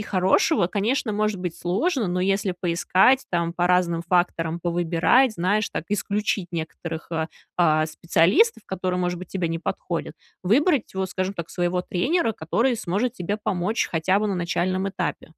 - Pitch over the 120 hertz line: Yes, medium, 185 Hz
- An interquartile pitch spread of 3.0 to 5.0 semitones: Yes, average, 3.3 semitones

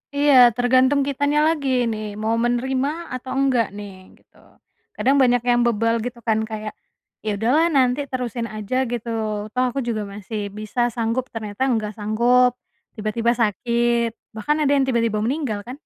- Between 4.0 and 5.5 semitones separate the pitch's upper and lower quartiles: No, average, 3.0 semitones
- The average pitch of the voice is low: No, high, 235 Hz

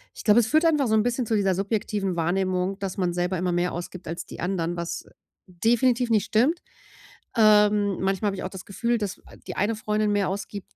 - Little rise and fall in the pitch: No, average, 3.2 semitones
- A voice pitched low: No, high, 200 Hz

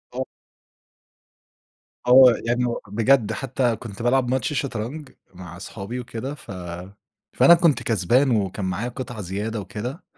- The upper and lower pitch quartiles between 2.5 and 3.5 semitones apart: No, average, 3.9 semitones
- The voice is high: No, low, 120 Hz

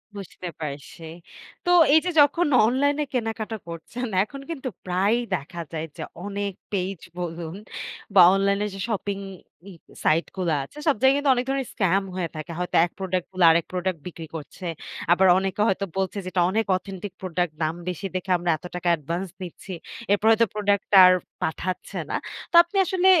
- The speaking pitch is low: No, high, 190 Hz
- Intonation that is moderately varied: Yes, average, 4.2 semitones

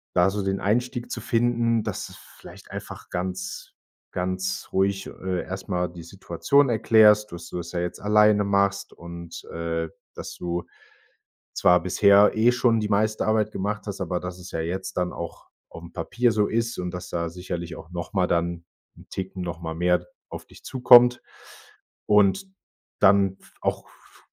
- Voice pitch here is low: Yes, very low, 95 Hz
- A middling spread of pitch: Yes, average, 3.3 semitones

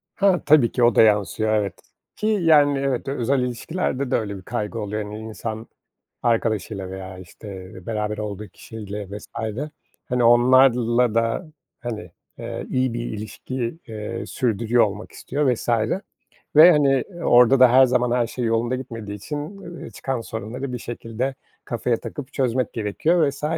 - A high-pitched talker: No, low, 120 Hz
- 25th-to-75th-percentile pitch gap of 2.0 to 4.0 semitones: Yes, average, 3.4 semitones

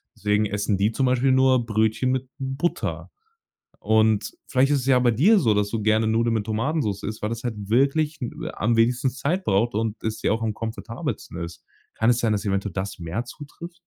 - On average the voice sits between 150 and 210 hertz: No, low, 115 Hz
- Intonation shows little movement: No, average, 3.6 semitones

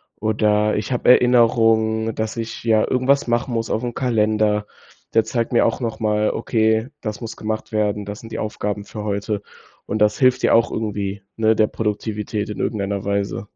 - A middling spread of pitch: No, narrow, 1.5 semitones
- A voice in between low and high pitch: No, low, 110 Hz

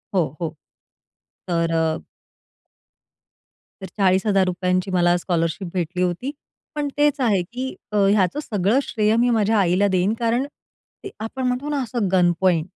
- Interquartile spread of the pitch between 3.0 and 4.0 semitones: No, average, 4.8 semitones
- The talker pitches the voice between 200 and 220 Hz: No, high, 190 Hz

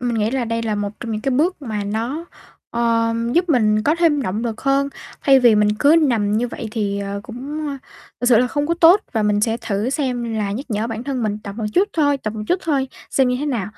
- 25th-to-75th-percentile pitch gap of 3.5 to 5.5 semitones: Yes, average, 4.6 semitones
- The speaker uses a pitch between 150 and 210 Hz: No, high, 235 Hz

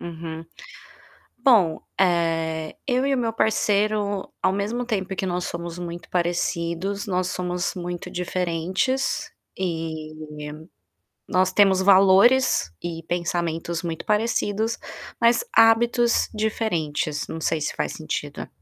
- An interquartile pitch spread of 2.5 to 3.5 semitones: No, average, 4.0 semitones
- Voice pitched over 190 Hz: No, medium, 185 Hz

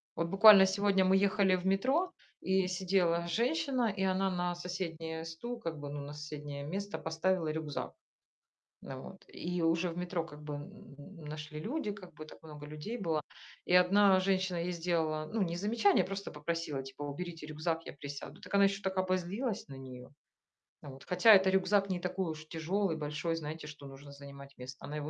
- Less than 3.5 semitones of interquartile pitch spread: No, average, 4.1 semitones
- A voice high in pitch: No, medium, 175 Hz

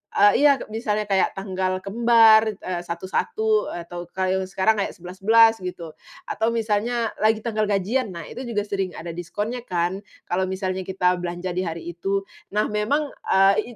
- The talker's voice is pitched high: Yes, high, 195 Hz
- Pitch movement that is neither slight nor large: Yes, average, 3.2 semitones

